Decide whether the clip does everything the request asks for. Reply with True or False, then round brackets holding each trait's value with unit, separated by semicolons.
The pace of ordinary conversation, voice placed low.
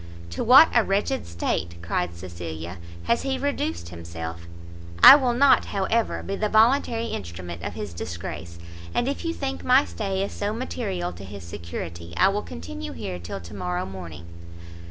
True (170 wpm; 95 Hz)